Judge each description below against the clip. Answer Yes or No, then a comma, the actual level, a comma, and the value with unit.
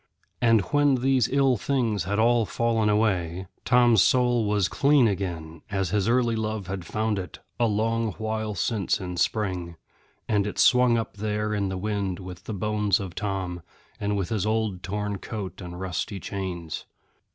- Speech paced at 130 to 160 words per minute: No, average, 170 wpm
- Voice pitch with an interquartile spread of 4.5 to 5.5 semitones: No, average, 3.2 semitones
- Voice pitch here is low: Yes, low, 105 Hz